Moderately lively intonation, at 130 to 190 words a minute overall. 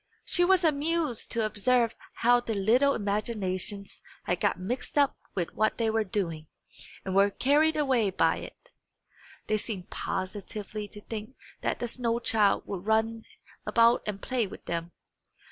Yes: average, 3.7 semitones; average, 155 wpm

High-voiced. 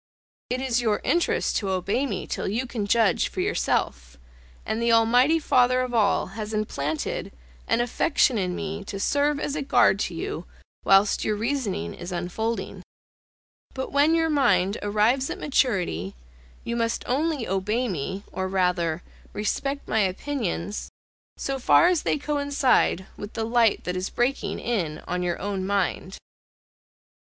Yes: high, 220 Hz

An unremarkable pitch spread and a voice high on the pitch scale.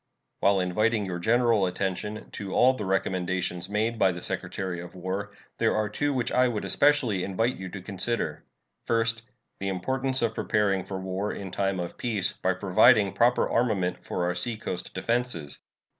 No: average, 3.8 semitones; low, 100 Hz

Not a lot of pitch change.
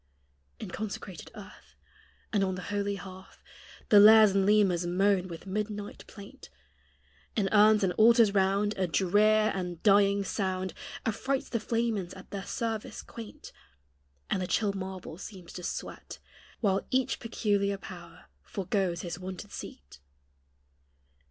Yes: narrow, 2.3 semitones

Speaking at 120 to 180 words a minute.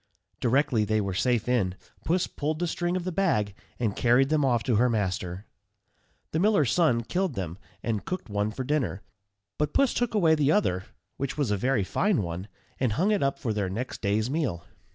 No: average, 200 wpm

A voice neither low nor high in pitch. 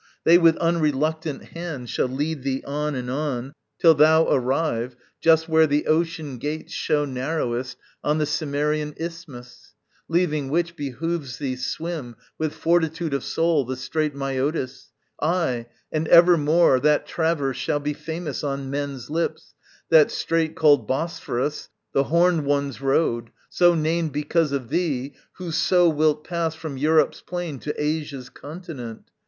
Yes: medium, 150 Hz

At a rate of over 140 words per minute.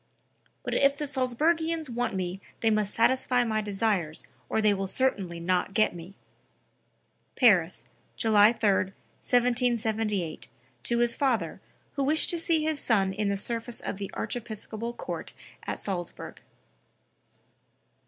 No: slow, 135 wpm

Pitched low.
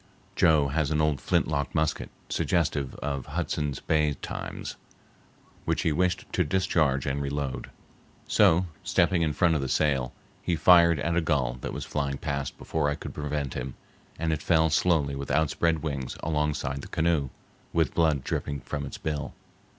Yes: very low, 75 Hz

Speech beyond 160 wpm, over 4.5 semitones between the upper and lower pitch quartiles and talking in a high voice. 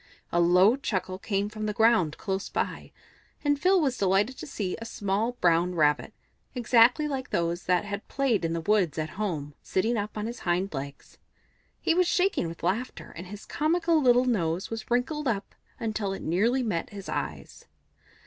Yes: average, 180 wpm; wide, 5.4 semitones; high, 210 Hz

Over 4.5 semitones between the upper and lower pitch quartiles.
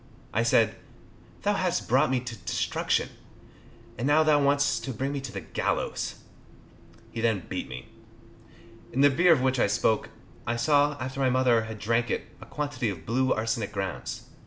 No: average, 3.9 semitones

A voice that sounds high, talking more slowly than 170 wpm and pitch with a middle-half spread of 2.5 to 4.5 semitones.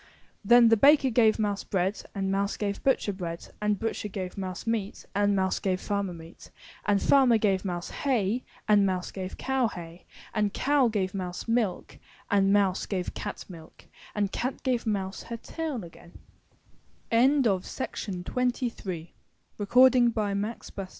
Yes: high, 200 Hz; average, 140 wpm; average, 3.2 semitones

